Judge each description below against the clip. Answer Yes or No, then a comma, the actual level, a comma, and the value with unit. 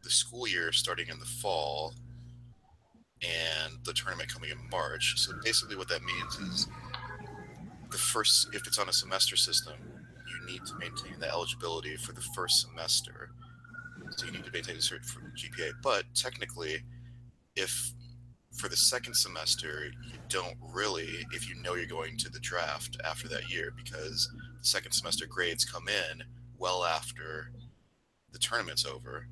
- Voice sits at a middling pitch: No, low, 120 Hz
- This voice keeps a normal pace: Yes, average, 160 wpm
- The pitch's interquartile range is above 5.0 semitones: Yes, wide, 5.5 semitones